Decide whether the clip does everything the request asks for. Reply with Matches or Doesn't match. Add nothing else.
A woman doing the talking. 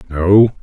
Doesn't match